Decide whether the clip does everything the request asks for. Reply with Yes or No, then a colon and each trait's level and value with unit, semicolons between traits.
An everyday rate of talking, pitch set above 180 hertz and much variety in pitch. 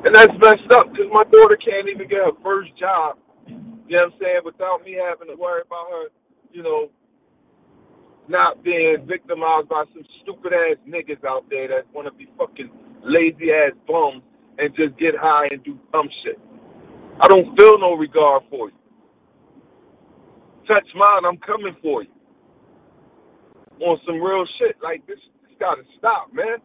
Yes: average, 175 wpm; high, 190 Hz; wide, 8.1 semitones